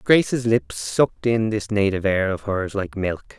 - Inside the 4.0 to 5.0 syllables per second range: Yes, 4.6 syllables/s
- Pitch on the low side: Yes, low, 105 Hz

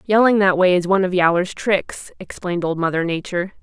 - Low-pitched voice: No, medium, 185 Hz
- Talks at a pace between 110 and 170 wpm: No, average, 200 wpm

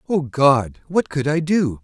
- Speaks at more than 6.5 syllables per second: No, 3.8 syllables/s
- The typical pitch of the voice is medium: Yes, medium, 145 Hz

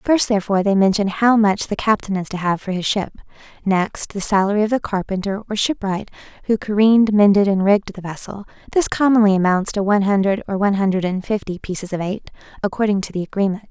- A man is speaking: No, female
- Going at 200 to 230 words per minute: Yes, fast, 205 wpm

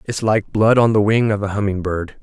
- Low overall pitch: Yes, low, 105 Hz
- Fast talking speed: Yes, fast, 270 wpm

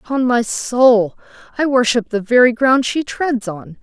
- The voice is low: No, high, 240 Hz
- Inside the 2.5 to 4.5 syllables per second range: Yes, 4.2 syllables/s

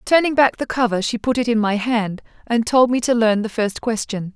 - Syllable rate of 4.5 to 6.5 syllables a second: Yes, 5.2 syllables/s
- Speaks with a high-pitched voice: Yes, high, 230 Hz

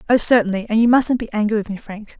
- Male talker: No, female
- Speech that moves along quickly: Yes, fast, 245 wpm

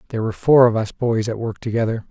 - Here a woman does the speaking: No, male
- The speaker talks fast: Yes, fast, 255 wpm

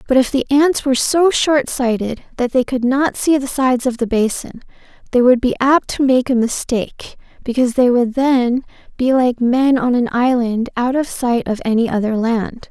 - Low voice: No, very high, 250 Hz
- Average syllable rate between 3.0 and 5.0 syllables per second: Yes, 4.9 syllables/s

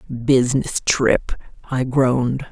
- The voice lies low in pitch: Yes, low, 130 Hz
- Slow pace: Yes, slow, 95 wpm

